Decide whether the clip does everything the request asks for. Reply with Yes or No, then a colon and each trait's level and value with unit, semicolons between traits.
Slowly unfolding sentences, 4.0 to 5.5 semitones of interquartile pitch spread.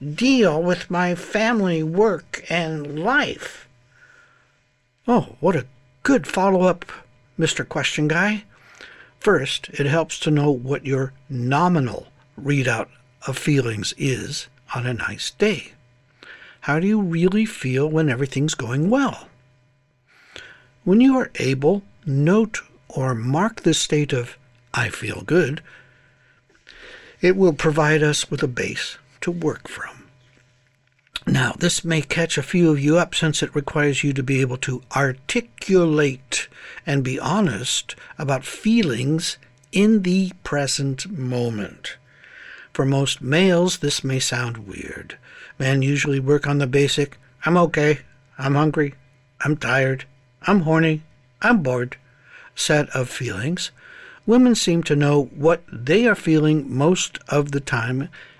Yes: slow, 130 wpm; average, 5.0 semitones